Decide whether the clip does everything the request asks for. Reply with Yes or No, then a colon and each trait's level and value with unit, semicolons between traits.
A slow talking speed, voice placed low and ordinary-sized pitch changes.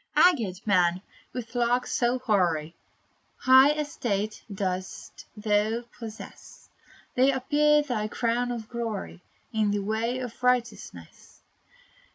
No: slow, 110 wpm; high, 230 Hz; average, 3.3 semitones